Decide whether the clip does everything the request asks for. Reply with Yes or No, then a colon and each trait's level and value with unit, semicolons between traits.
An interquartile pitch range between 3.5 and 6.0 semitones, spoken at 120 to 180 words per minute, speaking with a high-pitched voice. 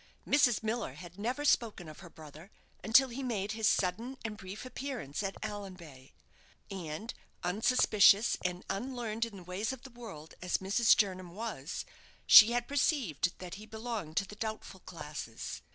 Yes: average, 4.6 semitones; average, 160 wpm; high, 210 Hz